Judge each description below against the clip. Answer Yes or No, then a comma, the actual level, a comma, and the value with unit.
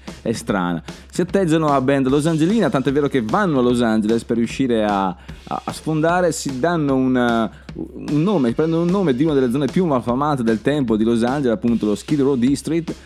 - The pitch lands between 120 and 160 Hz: Yes, medium, 140 Hz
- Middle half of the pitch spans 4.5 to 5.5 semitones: Yes, average, 5.2 semitones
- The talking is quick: Yes, fast, 200 wpm